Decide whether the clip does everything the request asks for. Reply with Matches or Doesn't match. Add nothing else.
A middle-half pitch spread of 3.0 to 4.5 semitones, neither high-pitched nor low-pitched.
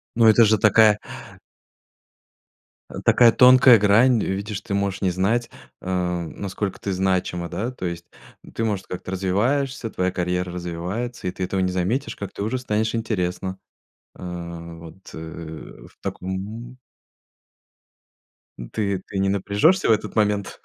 Doesn't match